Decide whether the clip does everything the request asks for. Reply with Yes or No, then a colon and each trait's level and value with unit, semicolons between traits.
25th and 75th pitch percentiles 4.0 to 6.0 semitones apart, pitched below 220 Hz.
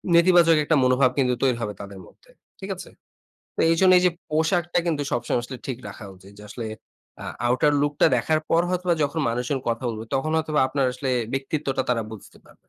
Yes: average, 4.7 semitones; low, 135 Hz